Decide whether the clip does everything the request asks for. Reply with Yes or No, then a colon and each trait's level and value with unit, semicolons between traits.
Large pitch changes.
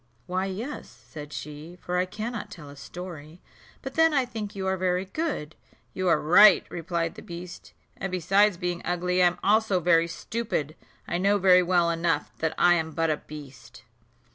No: average, 2.9 semitones